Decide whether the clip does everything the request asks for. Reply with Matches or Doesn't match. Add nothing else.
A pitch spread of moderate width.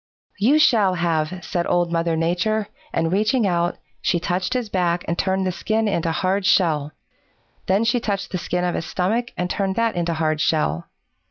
Matches